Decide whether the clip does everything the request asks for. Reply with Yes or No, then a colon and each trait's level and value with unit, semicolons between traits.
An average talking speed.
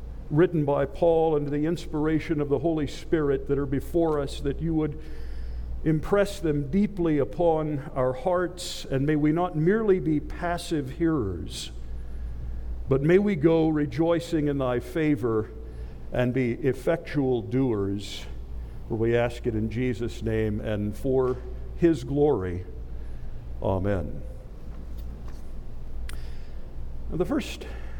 No: slow, 125 wpm